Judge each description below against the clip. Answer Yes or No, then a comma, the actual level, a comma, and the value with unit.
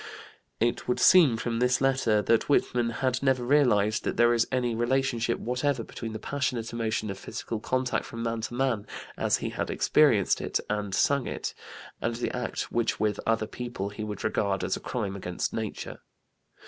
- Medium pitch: No, low, 115 Hz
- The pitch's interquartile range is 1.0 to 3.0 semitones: Yes, narrow, 2.5 semitones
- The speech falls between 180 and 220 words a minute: Yes, average, 185 wpm